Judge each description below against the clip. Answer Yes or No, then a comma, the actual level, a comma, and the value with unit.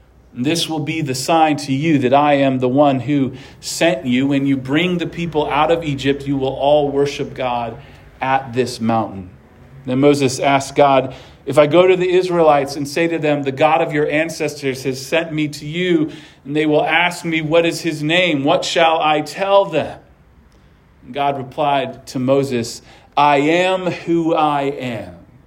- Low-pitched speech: No, medium, 145 Hz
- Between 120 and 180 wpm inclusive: No, average, 190 wpm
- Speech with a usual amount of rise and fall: Yes, average, 3.2 semitones